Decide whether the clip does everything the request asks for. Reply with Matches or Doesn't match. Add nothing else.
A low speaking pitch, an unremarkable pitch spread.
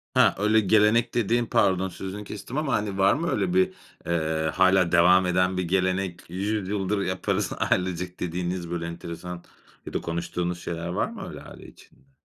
Matches